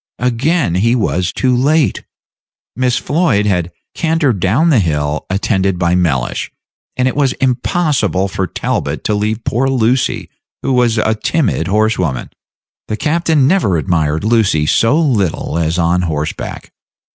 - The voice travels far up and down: Yes, wide, 6.6 semitones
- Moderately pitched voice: No, low, 110 Hz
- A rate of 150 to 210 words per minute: No, average, 140 wpm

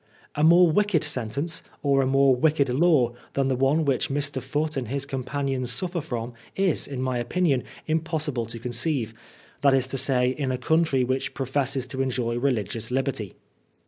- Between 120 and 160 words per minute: No, average, 175 wpm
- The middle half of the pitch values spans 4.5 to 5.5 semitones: No, average, 3.2 semitones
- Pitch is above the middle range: No, low, 135 Hz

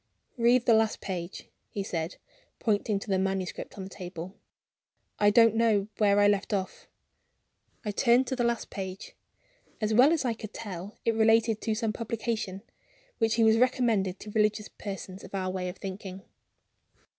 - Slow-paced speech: No, average, 170 wpm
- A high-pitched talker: Yes, high, 210 Hz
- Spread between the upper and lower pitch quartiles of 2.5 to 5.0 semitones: Yes, average, 3.0 semitones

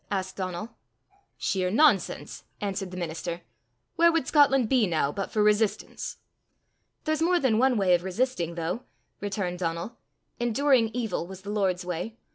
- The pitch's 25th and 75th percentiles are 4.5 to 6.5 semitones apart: Yes, wide, 5.5 semitones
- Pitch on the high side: Yes, high, 200 Hz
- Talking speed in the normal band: Yes, average, 150 wpm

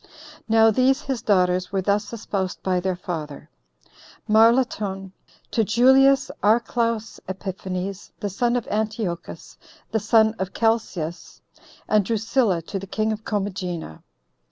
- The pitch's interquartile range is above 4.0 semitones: No, average, 3.3 semitones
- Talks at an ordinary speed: No, slow, 125 wpm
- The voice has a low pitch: No, high, 210 Hz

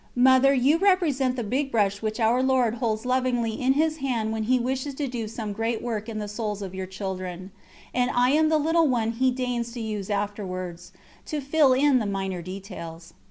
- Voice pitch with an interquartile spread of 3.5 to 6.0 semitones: Yes, average, 4.2 semitones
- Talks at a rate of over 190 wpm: Yes, fast, 205 wpm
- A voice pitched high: Yes, high, 235 Hz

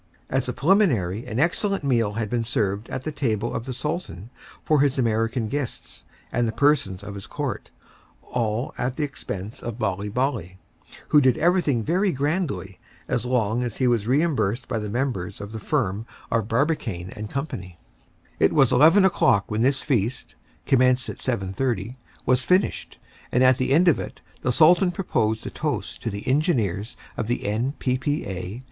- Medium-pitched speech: No, low, 125 Hz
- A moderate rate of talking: Yes, average, 180 wpm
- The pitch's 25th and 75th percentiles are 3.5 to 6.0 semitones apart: Yes, average, 4.9 semitones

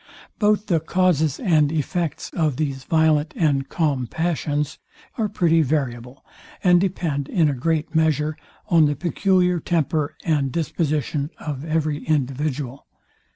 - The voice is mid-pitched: Yes, medium, 155 Hz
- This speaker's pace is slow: Yes, slow, 130 wpm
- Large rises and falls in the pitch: No, average, 2.7 semitones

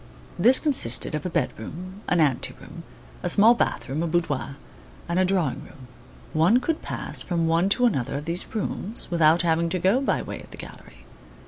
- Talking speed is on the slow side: No, average, 200 wpm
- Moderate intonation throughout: Yes, average, 4.0 semitones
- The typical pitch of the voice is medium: Yes, medium, 170 Hz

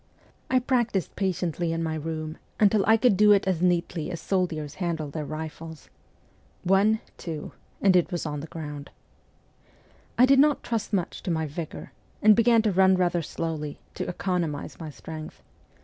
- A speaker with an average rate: Yes, average, 170 wpm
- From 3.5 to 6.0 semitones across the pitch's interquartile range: Yes, average, 4.1 semitones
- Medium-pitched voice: Yes, medium, 175 Hz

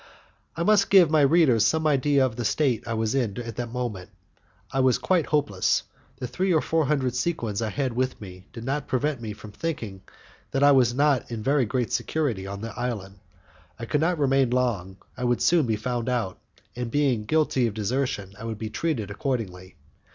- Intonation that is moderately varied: Yes, average, 4.6 semitones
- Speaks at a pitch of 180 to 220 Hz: No, low, 125 Hz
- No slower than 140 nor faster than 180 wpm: No, fast, 205 wpm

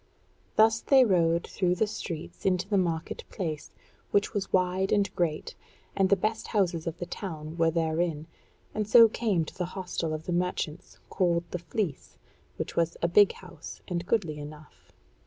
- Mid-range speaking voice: Yes, medium, 180 Hz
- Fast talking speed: No, average, 175 wpm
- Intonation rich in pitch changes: No, average, 3.2 semitones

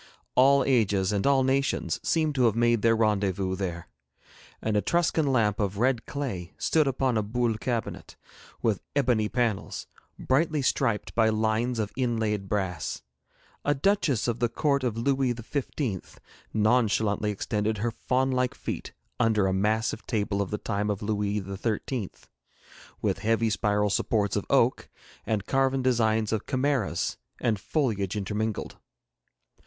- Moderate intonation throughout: Yes, average, 3.8 semitones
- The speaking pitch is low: Yes, low, 110 Hz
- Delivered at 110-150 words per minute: Yes, average, 145 wpm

